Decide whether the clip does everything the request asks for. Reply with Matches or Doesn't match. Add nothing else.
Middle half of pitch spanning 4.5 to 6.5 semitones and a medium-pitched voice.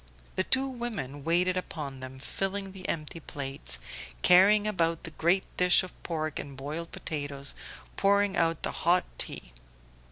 Matches